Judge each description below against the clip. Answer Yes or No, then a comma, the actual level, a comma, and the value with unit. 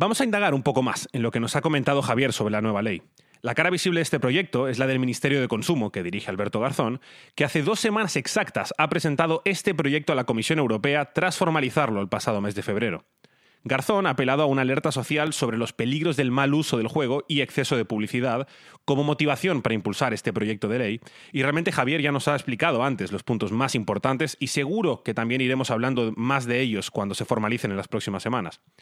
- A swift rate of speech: Yes, fast, 225 wpm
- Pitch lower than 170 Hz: Yes, low, 135 Hz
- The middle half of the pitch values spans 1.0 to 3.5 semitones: No, average, 4.6 semitones